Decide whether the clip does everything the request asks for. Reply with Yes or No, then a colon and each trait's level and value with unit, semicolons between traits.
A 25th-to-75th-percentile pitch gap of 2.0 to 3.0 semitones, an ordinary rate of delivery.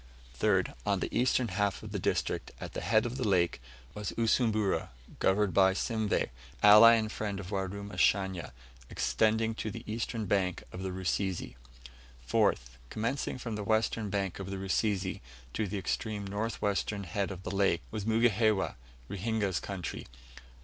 Yes: narrow, 2.5 semitones; average, 155 wpm